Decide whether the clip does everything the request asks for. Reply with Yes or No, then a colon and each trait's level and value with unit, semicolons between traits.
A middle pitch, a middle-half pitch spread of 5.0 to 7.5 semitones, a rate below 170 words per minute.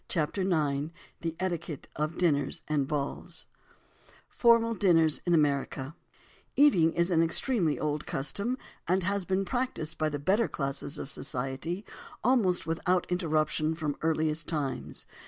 No: medium, 165 Hz; average, 3.8 semitones; average, 140 wpm